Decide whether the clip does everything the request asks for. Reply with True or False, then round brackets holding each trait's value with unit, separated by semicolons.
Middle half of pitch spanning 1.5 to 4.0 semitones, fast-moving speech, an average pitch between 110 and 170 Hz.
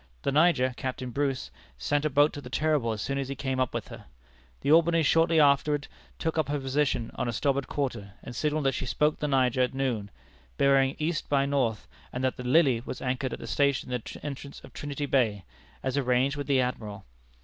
True (2.4 semitones; 215 wpm; 135 Hz)